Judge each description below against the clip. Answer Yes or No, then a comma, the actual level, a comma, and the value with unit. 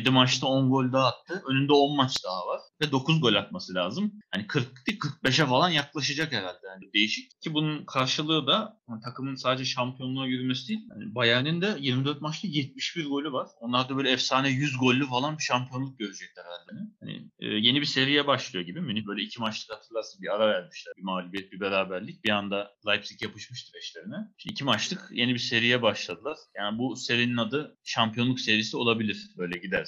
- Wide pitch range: No, average, 4.7 semitones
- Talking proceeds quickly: Yes, fast, 185 wpm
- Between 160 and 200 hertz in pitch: No, low, 130 Hz